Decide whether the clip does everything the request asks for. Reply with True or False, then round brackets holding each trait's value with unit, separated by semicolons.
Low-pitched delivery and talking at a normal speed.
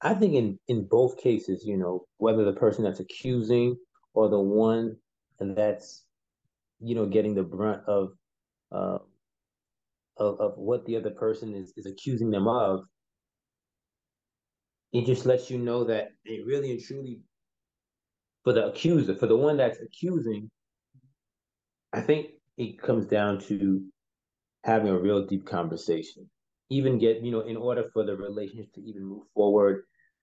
True (110 Hz; 155 wpm)